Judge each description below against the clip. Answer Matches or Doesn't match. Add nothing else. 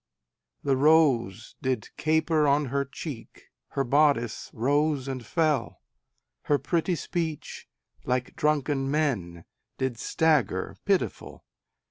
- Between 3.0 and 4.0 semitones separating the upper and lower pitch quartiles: Matches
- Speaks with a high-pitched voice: Doesn't match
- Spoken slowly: Matches